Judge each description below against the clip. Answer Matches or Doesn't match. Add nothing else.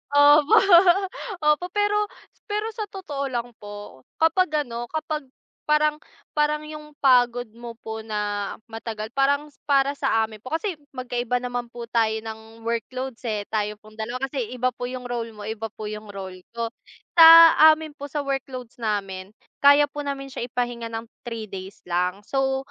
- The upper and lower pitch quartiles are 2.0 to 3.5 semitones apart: Doesn't match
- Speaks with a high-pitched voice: Matches